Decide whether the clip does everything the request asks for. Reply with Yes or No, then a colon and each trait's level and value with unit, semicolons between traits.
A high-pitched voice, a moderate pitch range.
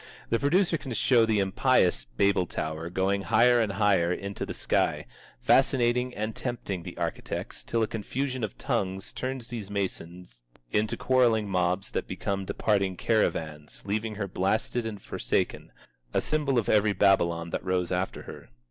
No: low, 100 Hz; average, 4.0 semitones